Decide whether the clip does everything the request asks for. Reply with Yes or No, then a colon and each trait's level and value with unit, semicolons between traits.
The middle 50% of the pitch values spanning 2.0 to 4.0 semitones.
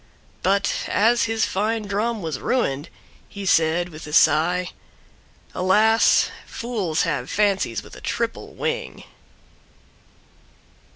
No: wide, 5.5 semitones